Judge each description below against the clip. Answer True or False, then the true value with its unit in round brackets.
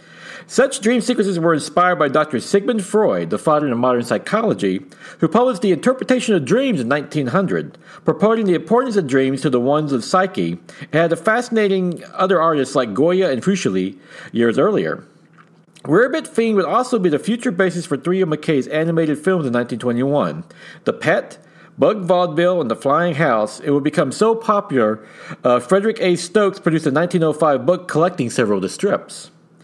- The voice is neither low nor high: True (175 Hz)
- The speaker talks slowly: False (170 wpm)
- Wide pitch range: True (5.9 semitones)